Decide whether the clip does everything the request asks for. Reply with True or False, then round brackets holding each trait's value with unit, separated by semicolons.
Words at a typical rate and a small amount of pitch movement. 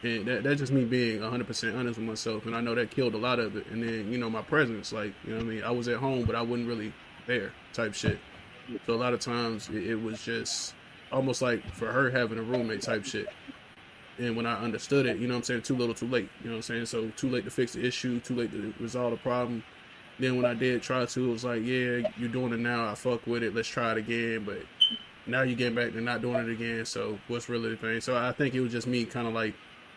False (275 wpm; 1.5 semitones)